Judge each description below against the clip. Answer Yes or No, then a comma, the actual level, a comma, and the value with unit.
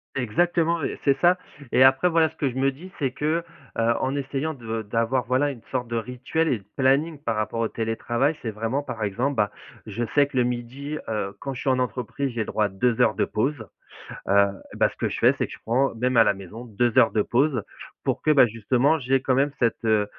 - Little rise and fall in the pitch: No, average, 3.8 semitones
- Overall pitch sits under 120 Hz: No, low, 125 Hz